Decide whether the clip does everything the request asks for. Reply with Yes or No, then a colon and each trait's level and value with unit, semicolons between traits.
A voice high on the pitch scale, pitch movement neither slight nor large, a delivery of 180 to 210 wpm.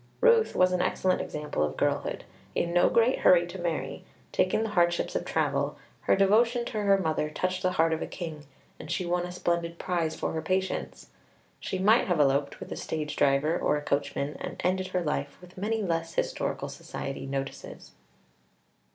No: medium, 175 Hz; average, 3.6 semitones; average, 185 wpm